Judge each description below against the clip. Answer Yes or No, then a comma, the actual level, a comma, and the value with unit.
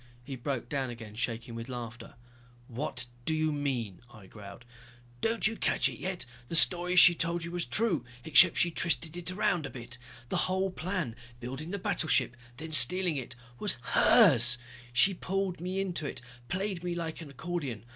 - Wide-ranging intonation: Yes, wide, 6.5 semitones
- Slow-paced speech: No, average, 175 wpm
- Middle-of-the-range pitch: Yes, medium, 160 Hz